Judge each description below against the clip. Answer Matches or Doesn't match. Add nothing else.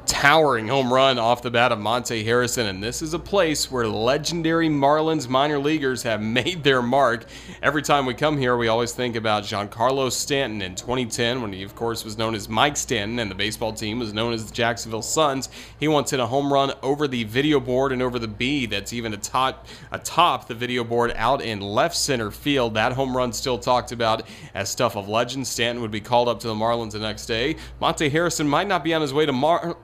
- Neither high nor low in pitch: Doesn't match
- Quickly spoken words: Matches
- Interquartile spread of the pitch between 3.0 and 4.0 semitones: Matches